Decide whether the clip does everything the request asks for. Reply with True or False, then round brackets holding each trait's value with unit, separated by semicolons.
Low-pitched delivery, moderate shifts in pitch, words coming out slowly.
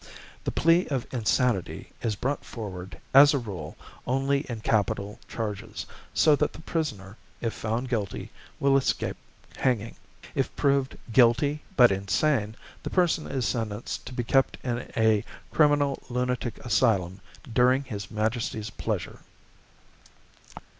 True (120 Hz; 4.3 semitones; 130 wpm)